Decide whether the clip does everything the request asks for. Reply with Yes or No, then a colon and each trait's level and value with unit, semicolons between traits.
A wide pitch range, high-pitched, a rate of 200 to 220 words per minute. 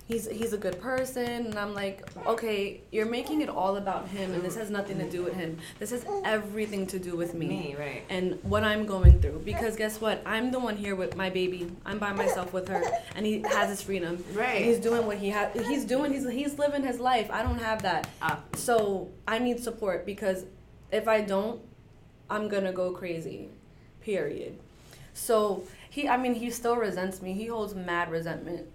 No: average, 3.8 semitones; high, 205 Hz; fast, 205 wpm